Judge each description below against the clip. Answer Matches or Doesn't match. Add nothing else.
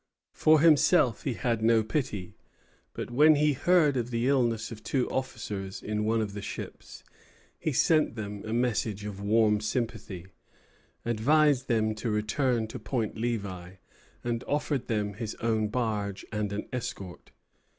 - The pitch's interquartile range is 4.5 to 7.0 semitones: Doesn't match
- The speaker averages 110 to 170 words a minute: Matches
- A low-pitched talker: Matches